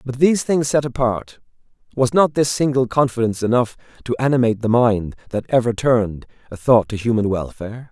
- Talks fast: No, average, 175 wpm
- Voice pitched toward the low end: Yes, low, 120 Hz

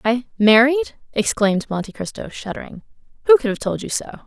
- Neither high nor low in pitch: No, high, 240 Hz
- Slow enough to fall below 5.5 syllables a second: No, 6.1 syllables/s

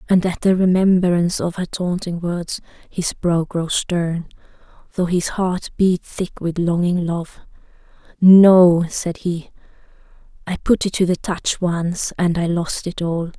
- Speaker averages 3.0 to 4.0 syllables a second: Yes, 3.9 syllables/s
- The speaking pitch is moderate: Yes, medium, 175 Hz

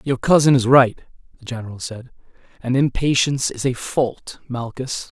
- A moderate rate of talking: Yes, average, 150 wpm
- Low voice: Yes, low, 125 Hz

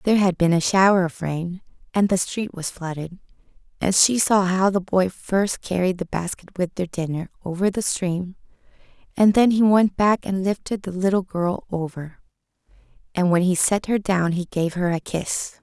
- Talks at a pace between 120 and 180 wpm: No, average, 190 wpm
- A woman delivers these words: Yes, female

